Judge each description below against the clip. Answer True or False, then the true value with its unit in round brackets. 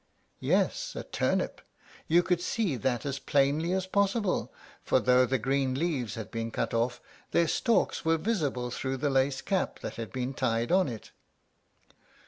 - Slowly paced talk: False (165 wpm)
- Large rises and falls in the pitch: True (6.0 semitones)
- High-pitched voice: False (135 Hz)